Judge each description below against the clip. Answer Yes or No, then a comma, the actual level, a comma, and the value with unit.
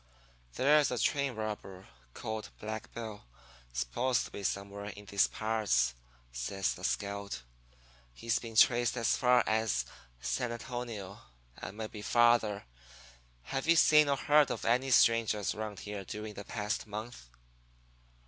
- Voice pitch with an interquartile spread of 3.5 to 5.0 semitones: No, average, 3.1 semitones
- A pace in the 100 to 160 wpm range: Yes, average, 140 wpm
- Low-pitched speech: Yes, low, 110 Hz